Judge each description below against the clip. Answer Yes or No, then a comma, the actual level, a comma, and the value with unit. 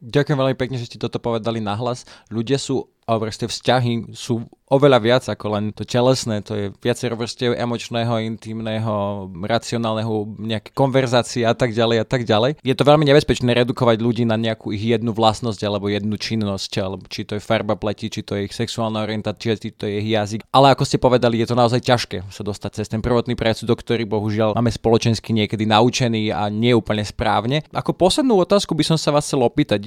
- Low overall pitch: Yes, low, 115 Hz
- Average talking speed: No, fast, 200 wpm